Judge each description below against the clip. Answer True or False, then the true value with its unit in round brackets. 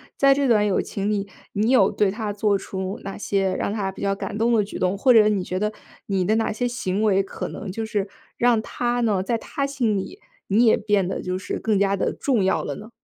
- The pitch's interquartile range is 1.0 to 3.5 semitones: True (2.6 semitones)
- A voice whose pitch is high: True (210 Hz)